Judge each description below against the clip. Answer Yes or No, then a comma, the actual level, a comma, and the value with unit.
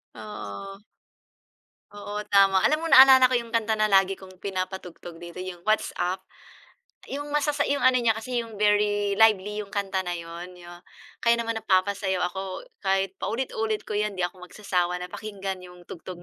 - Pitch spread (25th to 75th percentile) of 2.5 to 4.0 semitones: Yes, average, 3.3 semitones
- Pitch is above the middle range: Yes, high, 200 Hz